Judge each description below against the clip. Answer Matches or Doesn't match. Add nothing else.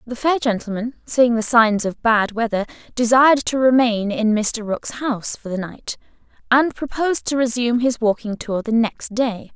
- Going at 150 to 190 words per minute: Matches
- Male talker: Doesn't match